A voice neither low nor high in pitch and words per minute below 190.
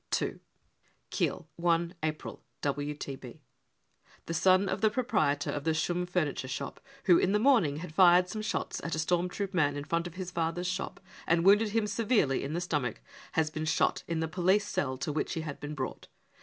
No: medium, 170 Hz; average, 200 wpm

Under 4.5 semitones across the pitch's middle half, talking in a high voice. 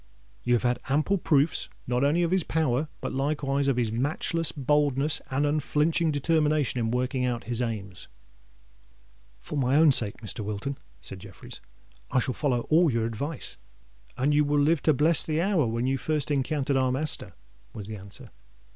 No: average, 3.8 semitones; medium, 140 Hz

